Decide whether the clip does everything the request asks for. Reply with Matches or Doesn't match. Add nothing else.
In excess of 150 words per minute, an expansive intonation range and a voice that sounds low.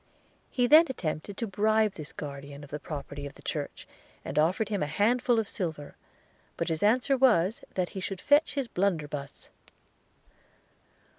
Doesn't match